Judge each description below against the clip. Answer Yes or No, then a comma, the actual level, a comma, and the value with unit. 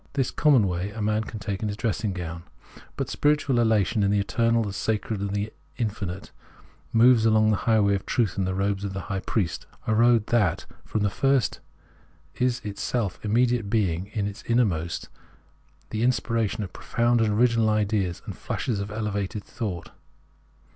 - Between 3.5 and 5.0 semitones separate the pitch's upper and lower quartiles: No, average, 2.7 semitones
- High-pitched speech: No, low, 105 Hz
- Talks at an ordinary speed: Yes, average, 180 wpm